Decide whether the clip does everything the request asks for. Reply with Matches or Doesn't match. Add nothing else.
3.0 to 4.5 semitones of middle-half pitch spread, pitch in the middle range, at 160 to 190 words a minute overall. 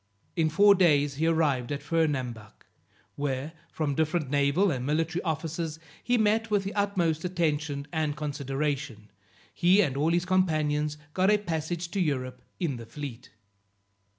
Doesn't match